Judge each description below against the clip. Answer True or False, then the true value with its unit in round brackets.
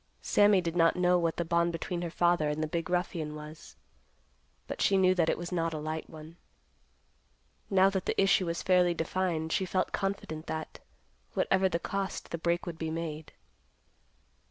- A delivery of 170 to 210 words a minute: True (180 wpm)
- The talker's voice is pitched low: False (170 Hz)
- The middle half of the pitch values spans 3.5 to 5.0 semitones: False (2.4 semitones)